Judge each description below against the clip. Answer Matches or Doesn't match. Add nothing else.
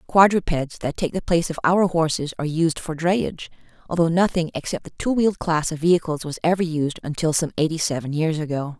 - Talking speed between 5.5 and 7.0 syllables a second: Matches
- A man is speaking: Doesn't match